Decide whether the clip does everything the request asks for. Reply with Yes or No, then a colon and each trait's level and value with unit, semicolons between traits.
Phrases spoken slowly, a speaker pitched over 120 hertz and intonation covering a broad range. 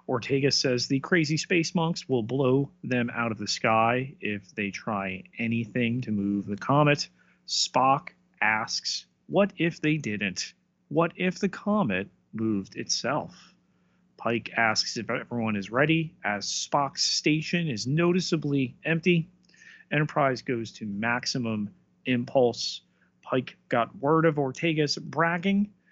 Yes: slow, 130 wpm; low, 135 Hz; wide, 6.3 semitones